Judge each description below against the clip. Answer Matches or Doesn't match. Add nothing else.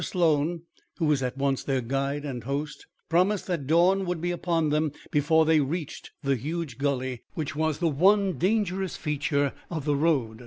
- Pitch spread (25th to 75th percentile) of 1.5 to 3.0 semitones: Doesn't match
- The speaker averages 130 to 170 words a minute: Doesn't match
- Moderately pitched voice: Matches